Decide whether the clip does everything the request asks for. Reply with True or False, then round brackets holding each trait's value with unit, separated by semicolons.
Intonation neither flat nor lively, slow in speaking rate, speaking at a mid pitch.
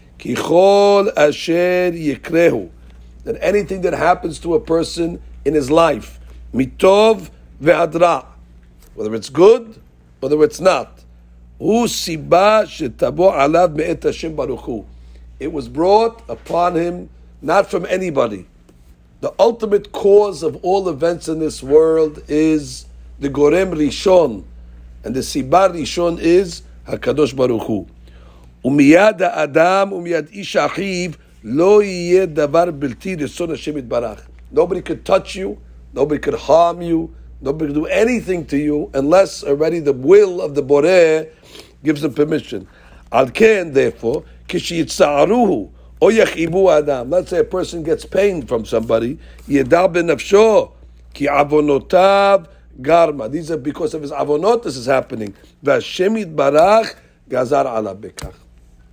False (8.1 semitones; 120 wpm; 155 Hz)